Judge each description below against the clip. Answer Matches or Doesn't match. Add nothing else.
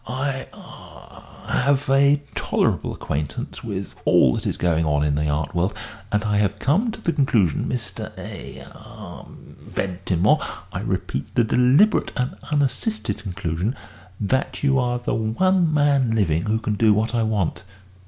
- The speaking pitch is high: Doesn't match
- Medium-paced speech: Matches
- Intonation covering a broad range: Matches